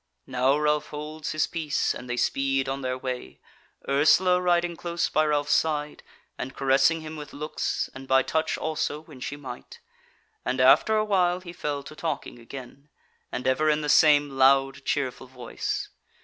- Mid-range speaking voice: Yes, medium, 145 Hz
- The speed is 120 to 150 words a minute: No, average, 170 wpm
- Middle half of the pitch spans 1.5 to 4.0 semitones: Yes, average, 2.9 semitones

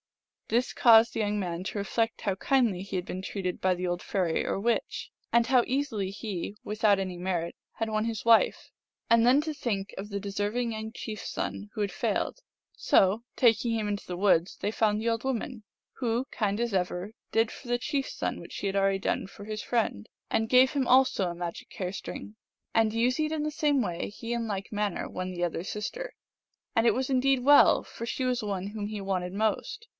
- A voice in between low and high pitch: No, high, 215 Hz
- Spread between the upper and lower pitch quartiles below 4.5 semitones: Yes, average, 3.6 semitones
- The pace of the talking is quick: Yes, fast, 220 wpm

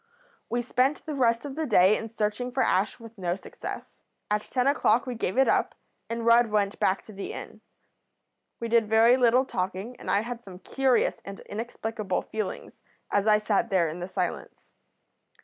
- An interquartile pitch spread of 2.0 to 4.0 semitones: Yes, average, 3.6 semitones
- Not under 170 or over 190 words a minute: Yes, average, 185 wpm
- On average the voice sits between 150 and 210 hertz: No, high, 225 Hz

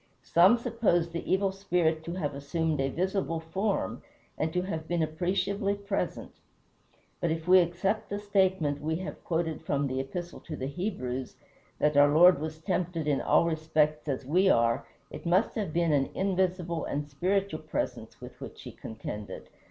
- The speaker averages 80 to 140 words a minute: No, average, 170 wpm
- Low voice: No, medium, 170 Hz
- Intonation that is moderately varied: Yes, average, 3.8 semitones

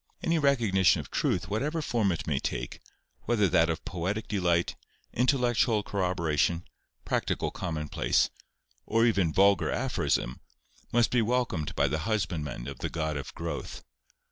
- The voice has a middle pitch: No, very low, 95 Hz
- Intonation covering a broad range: Yes, wide, 6.0 semitones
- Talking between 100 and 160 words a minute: Yes, average, 140 wpm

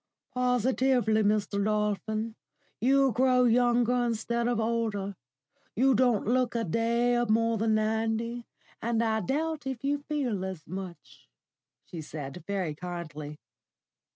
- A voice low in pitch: No, high, 230 Hz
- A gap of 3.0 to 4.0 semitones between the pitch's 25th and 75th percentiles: Yes, average, 3.3 semitones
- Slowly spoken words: Yes, slow, 125 wpm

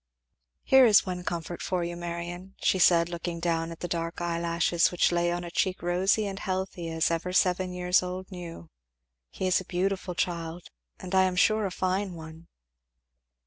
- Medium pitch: Yes, medium, 175 Hz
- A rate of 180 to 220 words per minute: Yes, average, 185 wpm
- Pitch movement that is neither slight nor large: No, narrow, 1.6 semitones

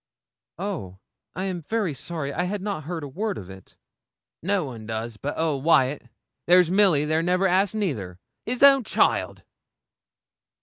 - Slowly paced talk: No, average, 150 wpm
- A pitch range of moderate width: No, wide, 6.0 semitones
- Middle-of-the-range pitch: Yes, medium, 170 Hz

